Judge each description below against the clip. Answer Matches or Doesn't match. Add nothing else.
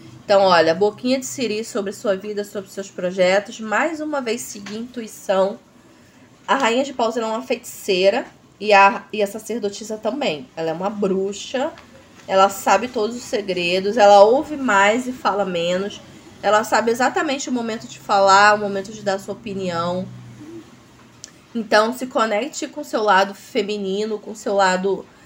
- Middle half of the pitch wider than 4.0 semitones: Doesn't match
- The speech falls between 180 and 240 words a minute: Doesn't match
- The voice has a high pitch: Matches